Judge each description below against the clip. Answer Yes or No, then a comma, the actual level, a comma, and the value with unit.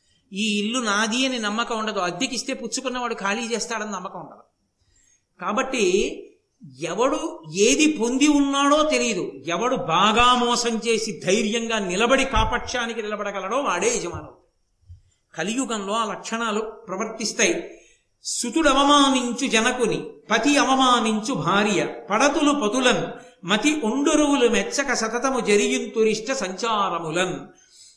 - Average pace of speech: Yes, average, 100 wpm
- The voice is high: Yes, high, 230 Hz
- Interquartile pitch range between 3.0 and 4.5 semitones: Yes, average, 3.9 semitones